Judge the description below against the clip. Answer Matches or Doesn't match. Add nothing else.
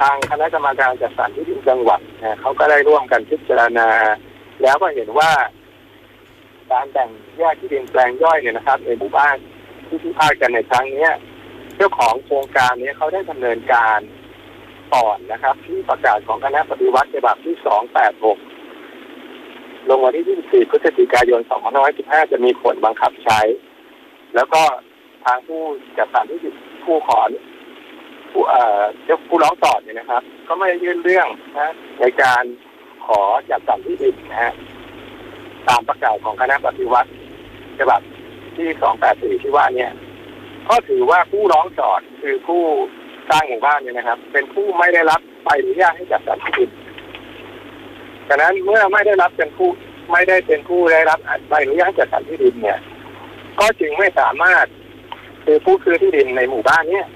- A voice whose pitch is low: Doesn't match